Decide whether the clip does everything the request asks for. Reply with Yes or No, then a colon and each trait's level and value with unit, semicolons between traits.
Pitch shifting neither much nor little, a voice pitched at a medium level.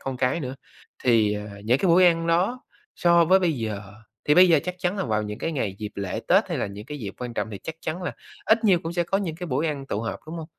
No: wide, 7.6 semitones; medium, 155 Hz